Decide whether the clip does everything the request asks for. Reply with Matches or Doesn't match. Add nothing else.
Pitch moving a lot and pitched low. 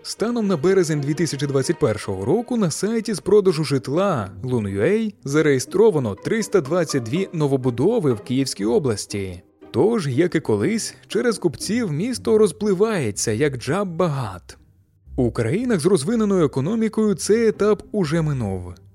Doesn't match